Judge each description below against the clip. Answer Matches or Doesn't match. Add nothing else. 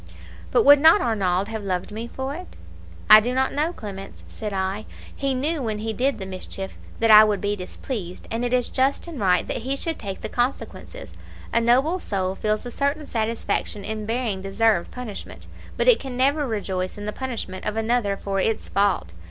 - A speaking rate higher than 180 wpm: Matches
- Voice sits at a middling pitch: Doesn't match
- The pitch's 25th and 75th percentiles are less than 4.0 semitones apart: Doesn't match